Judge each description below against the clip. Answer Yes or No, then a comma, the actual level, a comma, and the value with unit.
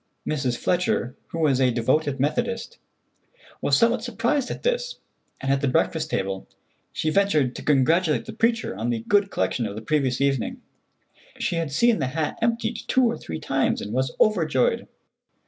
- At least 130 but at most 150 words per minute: No, average, 170 wpm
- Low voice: No, medium, 155 Hz